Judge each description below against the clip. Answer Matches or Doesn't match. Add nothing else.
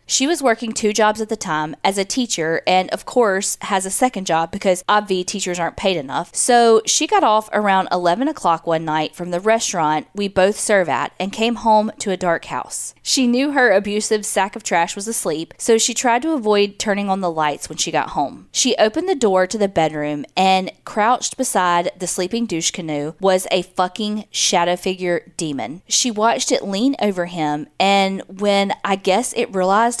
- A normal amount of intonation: Matches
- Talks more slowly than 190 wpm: Doesn't match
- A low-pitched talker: Doesn't match